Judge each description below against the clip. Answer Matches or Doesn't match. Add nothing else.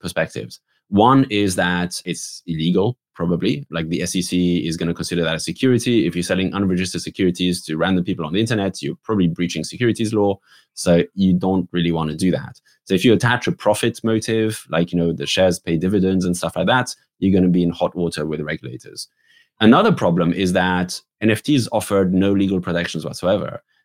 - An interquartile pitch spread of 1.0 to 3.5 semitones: Matches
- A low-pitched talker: Matches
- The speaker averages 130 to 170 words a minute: Doesn't match